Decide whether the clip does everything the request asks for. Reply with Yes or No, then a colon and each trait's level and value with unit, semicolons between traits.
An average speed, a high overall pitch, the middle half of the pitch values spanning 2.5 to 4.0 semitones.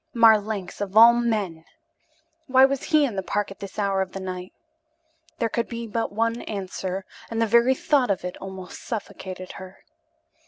Yes: average, 180 wpm; high, 210 Hz; average, 3.5 semitones